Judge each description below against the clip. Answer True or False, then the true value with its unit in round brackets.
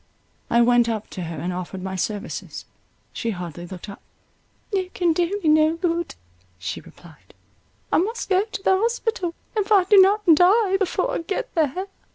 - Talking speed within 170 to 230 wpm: True (175 wpm)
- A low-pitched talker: False (335 Hz)